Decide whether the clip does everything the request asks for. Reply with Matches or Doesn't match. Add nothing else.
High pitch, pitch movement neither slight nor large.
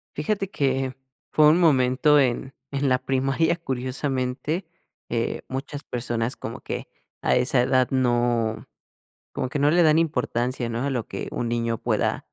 Doesn't match